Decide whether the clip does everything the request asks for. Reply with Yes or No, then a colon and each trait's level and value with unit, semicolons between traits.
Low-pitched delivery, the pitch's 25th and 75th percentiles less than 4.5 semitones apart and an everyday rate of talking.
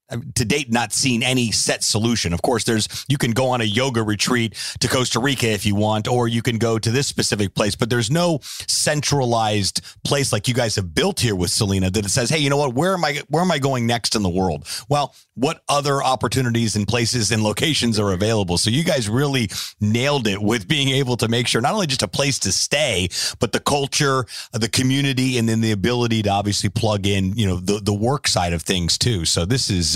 No: low, 120 Hz; average, 4.0 semitones; fast, 230 wpm